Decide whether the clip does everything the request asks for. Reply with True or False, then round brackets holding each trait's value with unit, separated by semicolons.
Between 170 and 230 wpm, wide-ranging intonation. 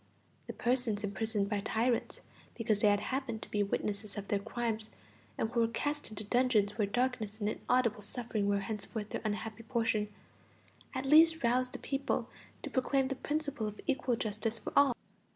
False (175 wpm; 3.3 semitones)